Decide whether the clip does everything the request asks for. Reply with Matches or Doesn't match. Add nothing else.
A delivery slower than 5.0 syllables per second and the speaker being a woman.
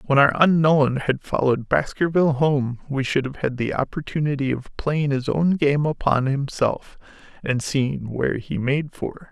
Doesn't match